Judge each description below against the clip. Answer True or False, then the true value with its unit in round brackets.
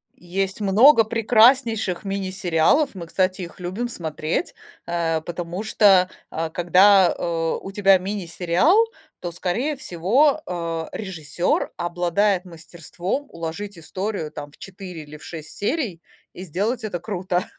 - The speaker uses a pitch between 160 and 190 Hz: True (185 Hz)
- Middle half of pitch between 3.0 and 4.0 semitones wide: True (3.4 semitones)